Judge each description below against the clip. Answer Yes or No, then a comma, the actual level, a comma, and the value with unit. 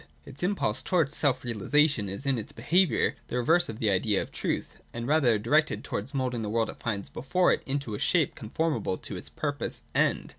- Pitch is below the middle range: Yes, low, 125 Hz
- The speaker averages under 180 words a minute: No, average, 200 wpm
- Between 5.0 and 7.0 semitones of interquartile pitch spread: Yes, wide, 5.4 semitones